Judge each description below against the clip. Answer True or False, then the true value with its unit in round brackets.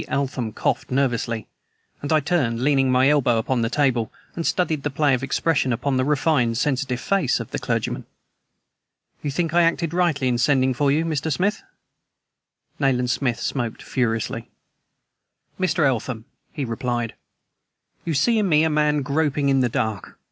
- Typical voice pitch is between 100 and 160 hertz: True (135 Hz)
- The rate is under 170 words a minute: True (160 wpm)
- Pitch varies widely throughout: False (3.6 semitones)